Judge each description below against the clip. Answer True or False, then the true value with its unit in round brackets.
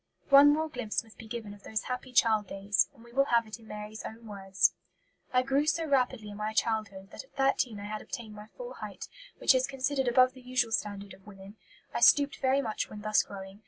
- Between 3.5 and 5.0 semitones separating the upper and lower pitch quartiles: True (3.9 semitones)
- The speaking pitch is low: False (225 Hz)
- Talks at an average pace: False (230 wpm)